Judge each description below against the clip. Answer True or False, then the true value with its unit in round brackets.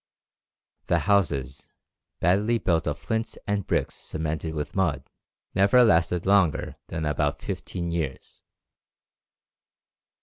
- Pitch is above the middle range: False (85 Hz)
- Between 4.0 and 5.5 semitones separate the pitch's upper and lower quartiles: True (4.8 semitones)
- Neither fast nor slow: False (105 wpm)